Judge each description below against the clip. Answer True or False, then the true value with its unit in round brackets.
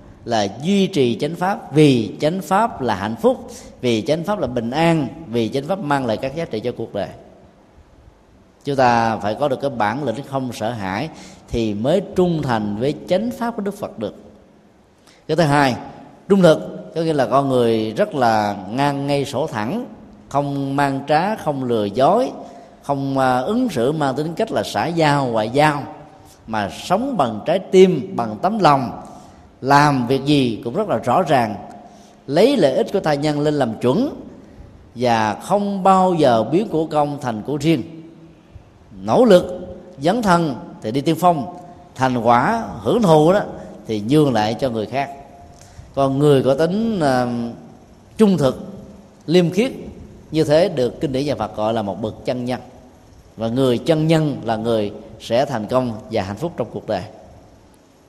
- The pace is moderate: True (180 wpm)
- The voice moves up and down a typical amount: False (6.0 semitones)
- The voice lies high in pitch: False (140 Hz)